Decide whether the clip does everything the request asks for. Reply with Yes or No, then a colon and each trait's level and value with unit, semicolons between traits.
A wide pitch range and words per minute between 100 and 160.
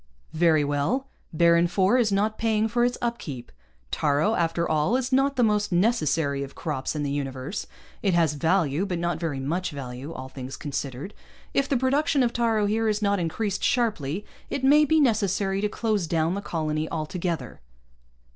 No: wide, 6.5 semitones; average, 175 wpm